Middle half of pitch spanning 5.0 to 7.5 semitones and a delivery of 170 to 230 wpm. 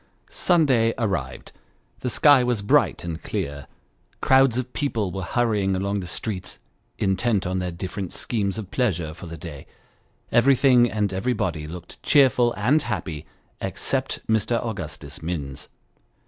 No: average, 5.3 semitones; slow, 135 wpm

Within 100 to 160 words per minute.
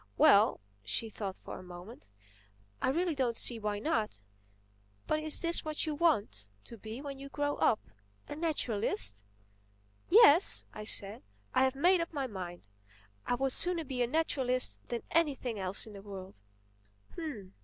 Yes: average, 150 wpm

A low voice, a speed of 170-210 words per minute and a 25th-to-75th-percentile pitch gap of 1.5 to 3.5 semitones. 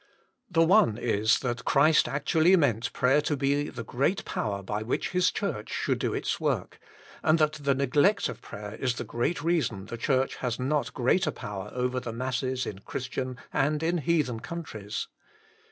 No: low, 130 Hz; average, 175 wpm; average, 4.6 semitones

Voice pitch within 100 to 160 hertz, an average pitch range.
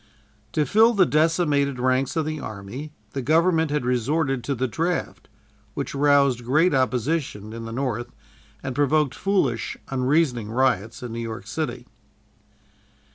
Yes: low, 135 Hz; average, 4.1 semitones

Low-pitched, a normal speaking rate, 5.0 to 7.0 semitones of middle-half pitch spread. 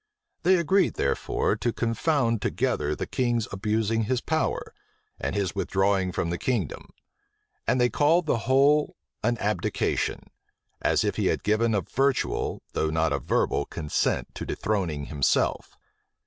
Yes: low, 115 Hz; average, 145 wpm; wide, 5.5 semitones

